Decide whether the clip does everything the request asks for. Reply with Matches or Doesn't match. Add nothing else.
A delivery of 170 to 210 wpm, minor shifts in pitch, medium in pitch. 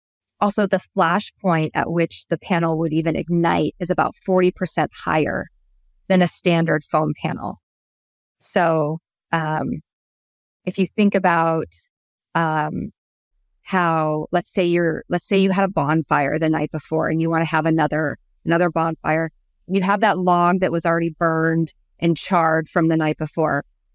Doesn't match